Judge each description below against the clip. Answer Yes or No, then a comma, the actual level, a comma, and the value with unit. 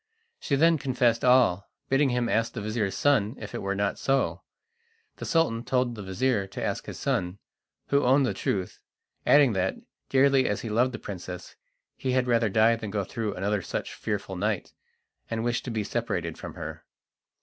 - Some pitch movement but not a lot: Yes, average, 4.3 semitones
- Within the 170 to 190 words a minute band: Yes, average, 185 wpm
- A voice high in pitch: No, low, 115 Hz